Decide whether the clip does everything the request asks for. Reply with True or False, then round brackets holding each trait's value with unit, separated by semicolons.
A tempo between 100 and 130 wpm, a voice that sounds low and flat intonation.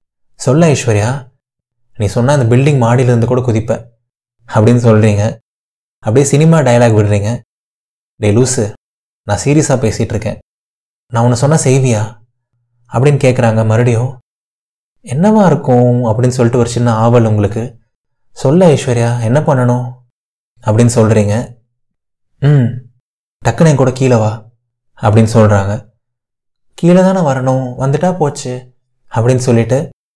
True (110 wpm; 120 Hz; 2.3 semitones)